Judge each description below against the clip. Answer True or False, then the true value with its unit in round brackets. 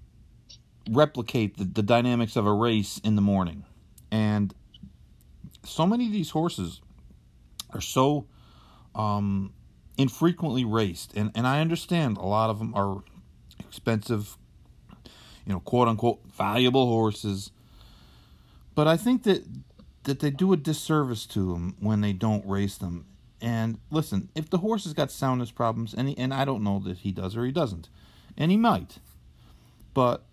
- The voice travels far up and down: True (6.2 semitones)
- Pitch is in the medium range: False (115 Hz)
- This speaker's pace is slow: False (155 wpm)